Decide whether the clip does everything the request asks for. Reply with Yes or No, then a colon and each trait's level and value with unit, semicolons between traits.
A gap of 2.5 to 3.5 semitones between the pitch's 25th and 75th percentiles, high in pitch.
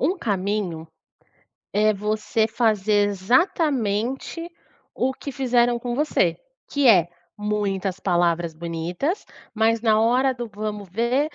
No: average, 4.1 semitones; high, 215 Hz